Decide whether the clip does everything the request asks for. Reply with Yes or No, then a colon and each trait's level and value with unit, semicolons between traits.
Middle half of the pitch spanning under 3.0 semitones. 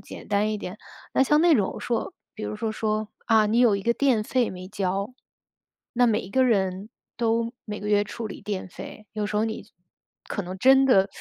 Yes: narrow, 2.6 semitones